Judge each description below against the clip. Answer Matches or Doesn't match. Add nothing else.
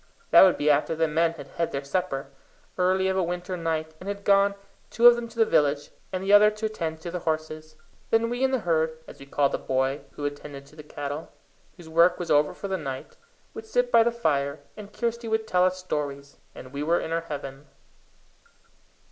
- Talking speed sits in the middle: Doesn't match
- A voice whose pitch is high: Doesn't match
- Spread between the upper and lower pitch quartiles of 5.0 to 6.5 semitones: Matches